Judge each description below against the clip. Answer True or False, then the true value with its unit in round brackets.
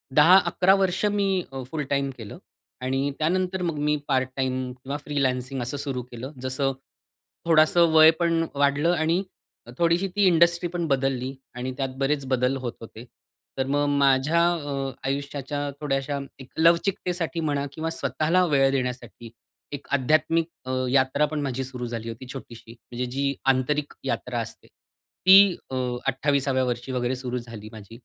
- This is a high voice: False (140 Hz)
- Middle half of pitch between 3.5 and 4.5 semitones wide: True (3.8 semitones)